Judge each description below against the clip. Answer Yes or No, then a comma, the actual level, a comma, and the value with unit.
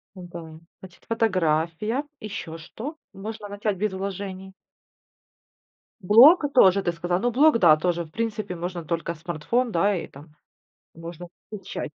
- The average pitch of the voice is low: No, high, 190 Hz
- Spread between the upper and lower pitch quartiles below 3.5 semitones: No, average, 4.1 semitones